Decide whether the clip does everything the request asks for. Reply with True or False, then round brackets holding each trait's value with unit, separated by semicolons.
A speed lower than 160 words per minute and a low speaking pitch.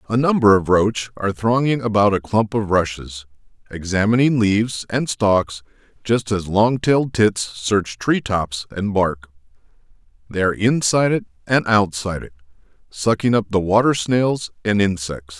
True (150 wpm; 105 Hz)